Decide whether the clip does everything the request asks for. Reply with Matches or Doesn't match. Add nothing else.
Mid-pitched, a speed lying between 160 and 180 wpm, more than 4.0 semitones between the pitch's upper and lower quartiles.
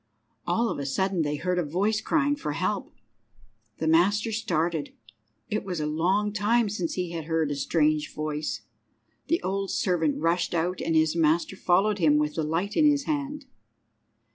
Matches